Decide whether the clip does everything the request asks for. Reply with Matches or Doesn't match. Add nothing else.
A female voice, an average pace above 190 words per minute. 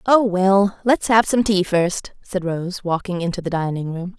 Matches